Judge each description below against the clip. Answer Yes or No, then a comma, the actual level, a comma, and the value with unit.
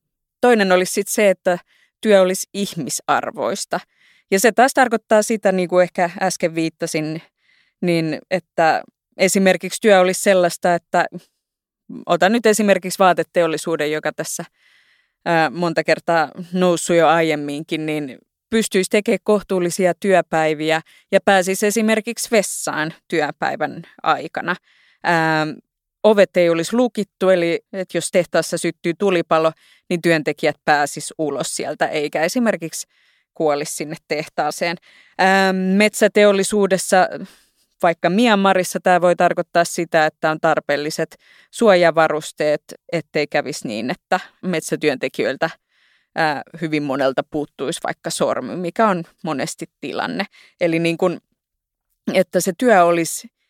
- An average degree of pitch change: Yes, average, 3.3 semitones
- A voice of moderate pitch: Yes, medium, 175 Hz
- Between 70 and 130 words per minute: Yes, average, 115 wpm